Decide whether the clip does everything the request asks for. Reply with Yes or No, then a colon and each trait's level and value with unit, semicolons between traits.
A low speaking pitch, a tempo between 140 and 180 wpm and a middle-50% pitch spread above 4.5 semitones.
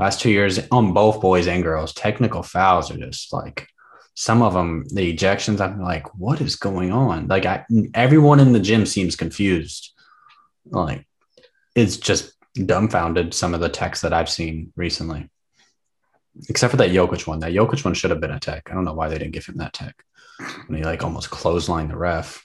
No: very low, 95 Hz; average, 200 wpm; average, 5.1 semitones